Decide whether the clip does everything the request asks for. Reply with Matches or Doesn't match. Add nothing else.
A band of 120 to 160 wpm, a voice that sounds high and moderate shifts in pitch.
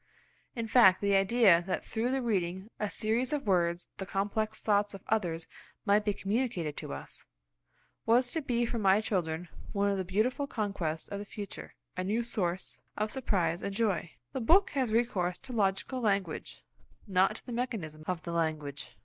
Doesn't match